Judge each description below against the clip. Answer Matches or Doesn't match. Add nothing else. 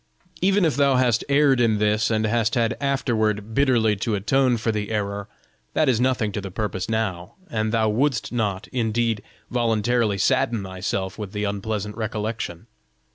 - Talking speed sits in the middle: Matches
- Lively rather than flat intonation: Doesn't match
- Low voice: Matches